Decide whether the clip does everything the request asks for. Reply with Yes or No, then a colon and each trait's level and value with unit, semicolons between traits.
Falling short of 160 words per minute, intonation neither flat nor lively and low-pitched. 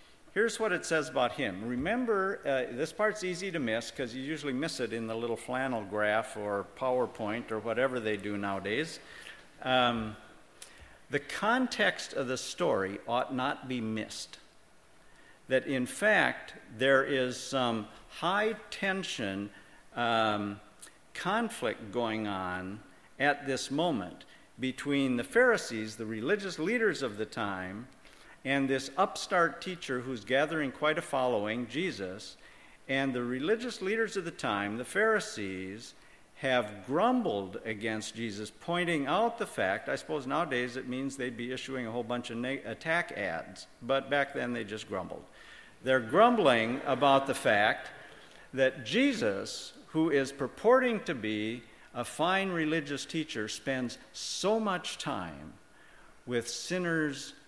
No: average, 140 wpm; wide, 7.0 semitones; low, 130 Hz